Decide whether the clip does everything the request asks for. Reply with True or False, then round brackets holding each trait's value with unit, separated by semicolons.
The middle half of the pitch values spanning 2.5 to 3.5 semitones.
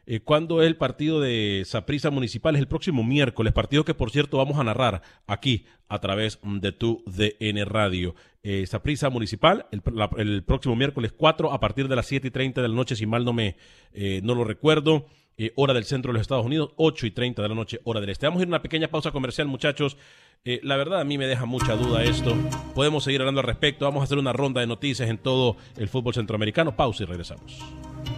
False (4.5 semitones)